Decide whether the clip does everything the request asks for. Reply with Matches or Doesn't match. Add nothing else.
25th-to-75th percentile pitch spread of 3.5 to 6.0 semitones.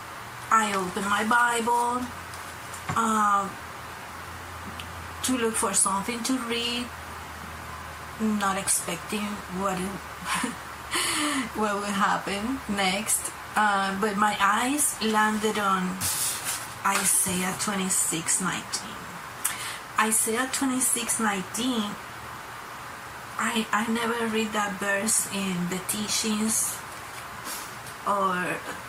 Doesn't match